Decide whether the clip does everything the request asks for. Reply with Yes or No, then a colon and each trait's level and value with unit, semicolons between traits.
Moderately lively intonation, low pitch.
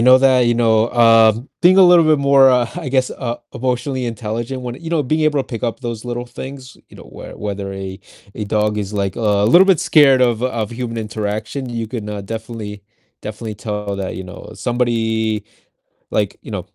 Yes: average, 3.4 semitones; low, 115 Hz